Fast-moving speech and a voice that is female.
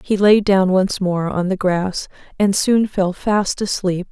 No: average, 190 wpm; female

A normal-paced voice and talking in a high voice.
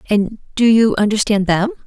Yes: average, 160 wpm; high, 215 Hz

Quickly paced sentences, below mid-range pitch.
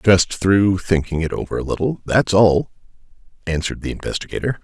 No: average, 155 wpm; very low, 95 Hz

